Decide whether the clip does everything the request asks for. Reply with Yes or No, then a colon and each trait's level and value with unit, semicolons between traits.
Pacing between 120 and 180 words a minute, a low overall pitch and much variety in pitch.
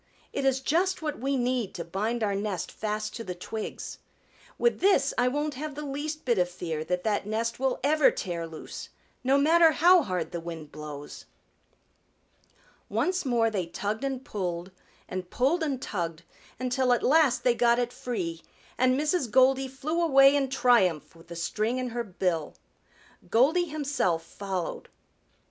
No: average, 165 wpm; high, 240 Hz; wide, 7.1 semitones